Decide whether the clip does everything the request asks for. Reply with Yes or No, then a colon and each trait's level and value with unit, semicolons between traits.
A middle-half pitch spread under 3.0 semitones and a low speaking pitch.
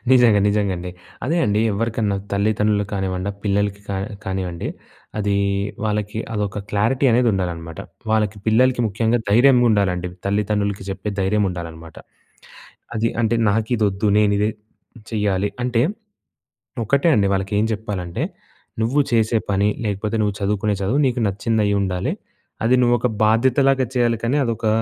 Yes: narrow, 2.5 semitones; low, 105 Hz